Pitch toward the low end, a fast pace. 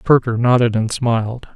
No: low, 120 Hz; average, 155 wpm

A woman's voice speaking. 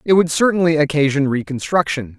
No: male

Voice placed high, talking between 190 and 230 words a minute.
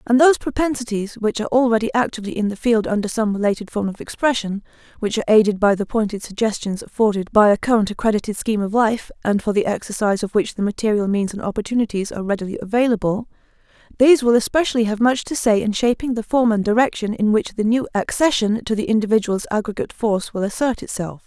Yes: high, 220 Hz; average, 195 wpm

